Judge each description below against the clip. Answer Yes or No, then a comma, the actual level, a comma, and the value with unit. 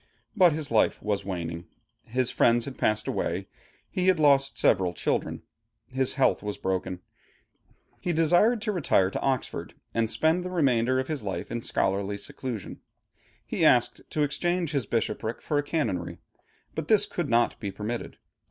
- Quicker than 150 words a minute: Yes, average, 160 wpm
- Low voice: Yes, low, 130 Hz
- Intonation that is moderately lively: No, wide, 7.2 semitones